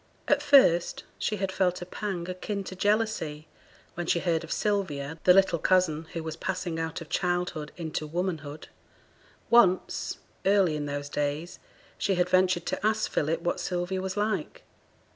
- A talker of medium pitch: Yes, medium, 180 Hz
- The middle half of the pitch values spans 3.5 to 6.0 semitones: No, average, 3.1 semitones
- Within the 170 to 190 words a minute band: No, average, 160 wpm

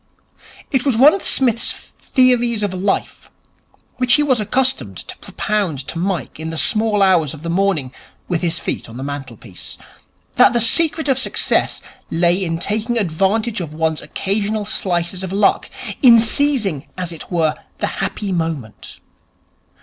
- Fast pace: No, average, 155 wpm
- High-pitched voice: Yes, high, 195 Hz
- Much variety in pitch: Yes, wide, 6.0 semitones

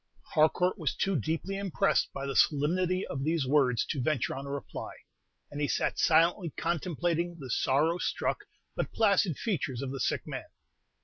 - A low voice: No, medium, 155 Hz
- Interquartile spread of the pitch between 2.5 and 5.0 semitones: Yes, average, 4.2 semitones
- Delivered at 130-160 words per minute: No, average, 170 wpm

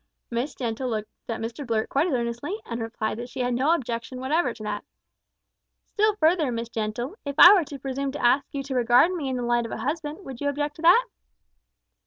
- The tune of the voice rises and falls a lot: No, average, 4.0 semitones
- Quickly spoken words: Yes, fast, 225 wpm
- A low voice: No, very high, 260 Hz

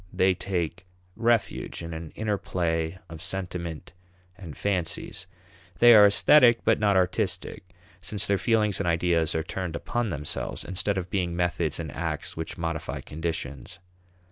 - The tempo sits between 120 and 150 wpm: Yes, average, 145 wpm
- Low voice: Yes, very low, 90 Hz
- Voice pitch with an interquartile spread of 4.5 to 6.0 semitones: No, average, 3.3 semitones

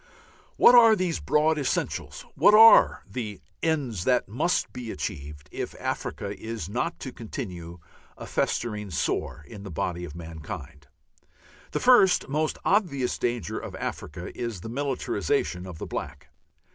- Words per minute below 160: Yes, average, 145 wpm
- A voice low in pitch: Yes, low, 115 Hz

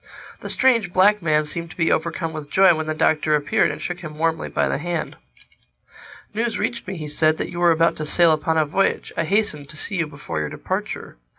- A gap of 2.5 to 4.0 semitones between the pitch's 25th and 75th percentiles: Yes, average, 2.9 semitones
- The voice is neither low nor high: Yes, medium, 165 Hz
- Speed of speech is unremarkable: No, fast, 225 wpm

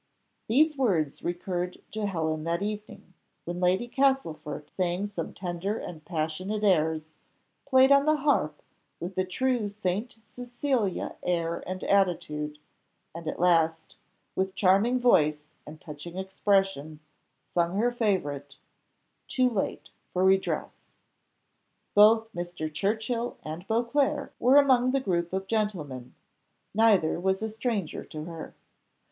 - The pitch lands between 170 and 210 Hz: Yes, high, 190 Hz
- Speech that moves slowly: Yes, slow, 125 wpm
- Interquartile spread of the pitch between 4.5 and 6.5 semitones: Yes, average, 5.2 semitones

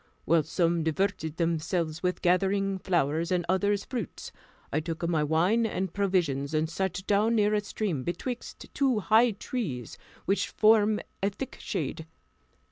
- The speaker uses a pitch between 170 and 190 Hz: Yes, medium, 185 Hz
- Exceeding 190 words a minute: No, average, 145 wpm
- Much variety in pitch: No, average, 4.1 semitones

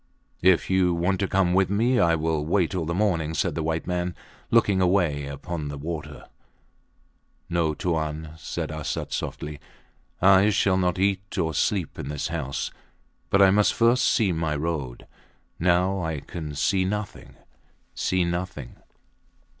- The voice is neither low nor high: No, very low, 85 Hz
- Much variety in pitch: No, average, 3.5 semitones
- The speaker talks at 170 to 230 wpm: No, average, 155 wpm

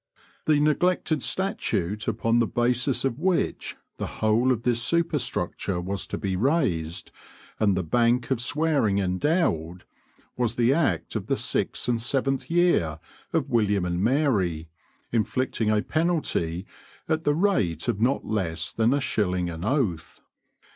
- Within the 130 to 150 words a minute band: Yes, average, 145 wpm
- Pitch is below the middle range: Yes, low, 115 Hz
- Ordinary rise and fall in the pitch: No, wide, 7.4 semitones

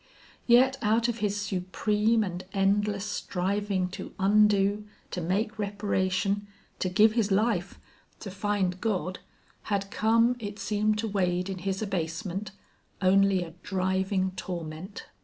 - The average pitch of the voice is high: Yes, high, 200 Hz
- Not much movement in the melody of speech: Yes, narrow, 2.1 semitones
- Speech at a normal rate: No, slow, 130 wpm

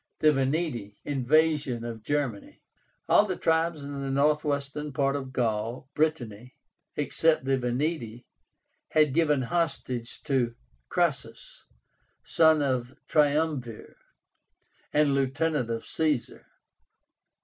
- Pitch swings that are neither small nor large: Yes, average, 3.7 semitones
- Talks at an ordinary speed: No, slow, 105 wpm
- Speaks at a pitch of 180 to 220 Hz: No, medium, 140 Hz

